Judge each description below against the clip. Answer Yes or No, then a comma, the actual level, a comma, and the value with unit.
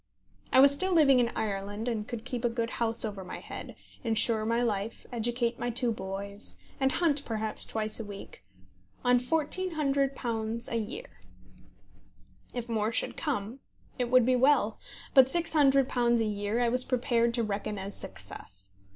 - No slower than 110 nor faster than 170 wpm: Yes, average, 160 wpm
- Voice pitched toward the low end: No, high, 235 Hz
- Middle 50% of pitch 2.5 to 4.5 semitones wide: Yes, average, 3.0 semitones